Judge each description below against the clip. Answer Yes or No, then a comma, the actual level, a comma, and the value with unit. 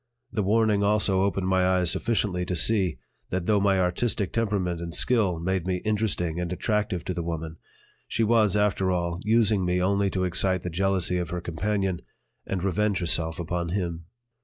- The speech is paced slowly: No, average, 180 wpm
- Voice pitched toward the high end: No, very low, 95 Hz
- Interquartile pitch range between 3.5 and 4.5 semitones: No, average, 2.8 semitones